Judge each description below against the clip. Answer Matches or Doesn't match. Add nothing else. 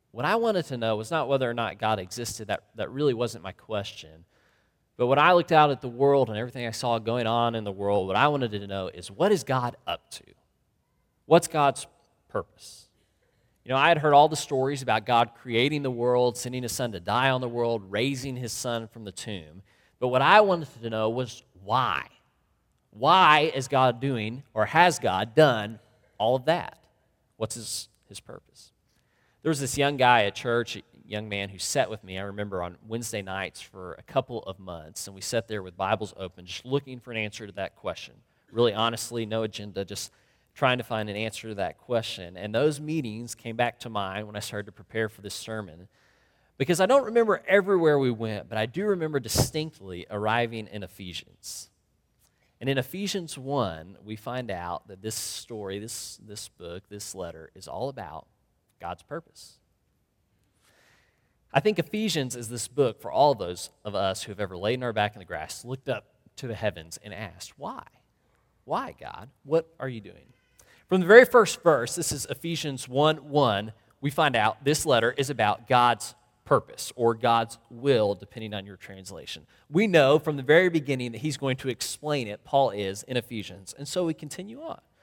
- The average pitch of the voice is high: Doesn't match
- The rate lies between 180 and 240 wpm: Matches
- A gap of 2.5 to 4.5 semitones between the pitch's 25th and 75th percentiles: Doesn't match